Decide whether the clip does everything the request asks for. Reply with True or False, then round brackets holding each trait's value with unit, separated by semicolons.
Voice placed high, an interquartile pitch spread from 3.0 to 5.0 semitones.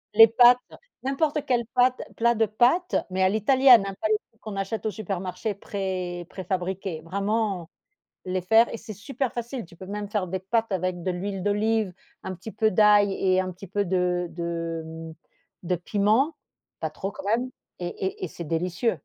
True (200 Hz; 3.7 semitones)